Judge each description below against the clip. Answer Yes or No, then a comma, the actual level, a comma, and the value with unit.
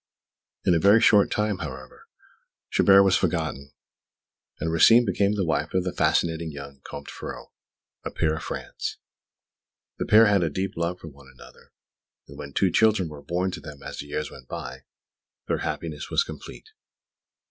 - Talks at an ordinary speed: Yes, average, 170 wpm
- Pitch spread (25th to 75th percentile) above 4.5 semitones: Yes, average, 5.2 semitones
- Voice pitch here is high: No, very low, 85 Hz